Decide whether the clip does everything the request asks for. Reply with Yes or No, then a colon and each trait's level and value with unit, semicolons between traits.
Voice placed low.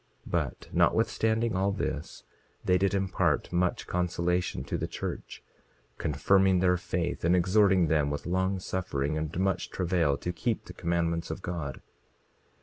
Yes: very low, 90 Hz